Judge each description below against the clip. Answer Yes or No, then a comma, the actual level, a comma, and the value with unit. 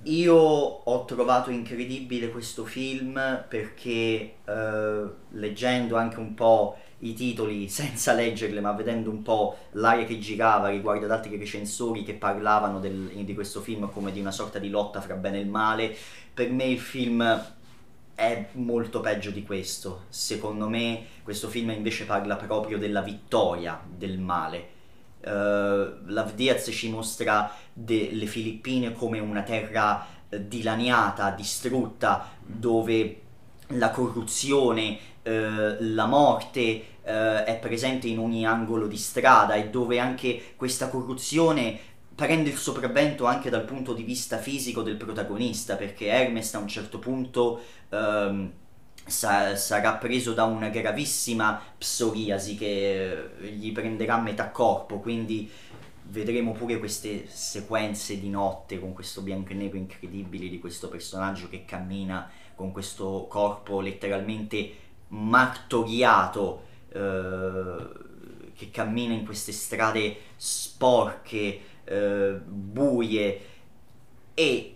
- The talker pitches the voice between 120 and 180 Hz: No, low, 110 Hz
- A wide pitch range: No, narrow, 2.6 semitones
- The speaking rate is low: No, average, 125 wpm